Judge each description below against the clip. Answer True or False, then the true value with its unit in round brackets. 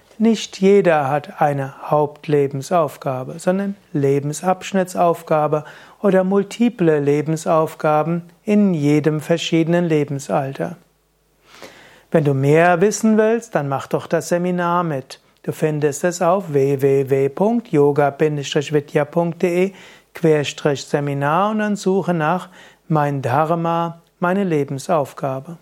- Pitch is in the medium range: True (160 Hz)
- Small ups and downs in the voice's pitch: False (3.8 semitones)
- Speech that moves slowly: True (95 wpm)